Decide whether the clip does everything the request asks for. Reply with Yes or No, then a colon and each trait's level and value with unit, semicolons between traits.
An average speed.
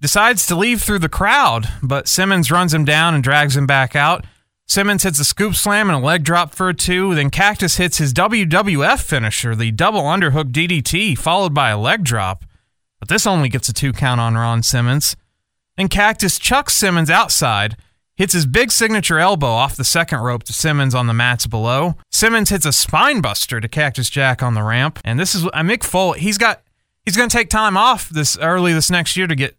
No: fast, 215 wpm